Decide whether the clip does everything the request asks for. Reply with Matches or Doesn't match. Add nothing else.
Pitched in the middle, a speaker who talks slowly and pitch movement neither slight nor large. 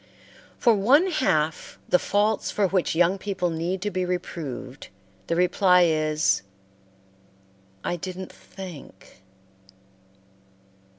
Matches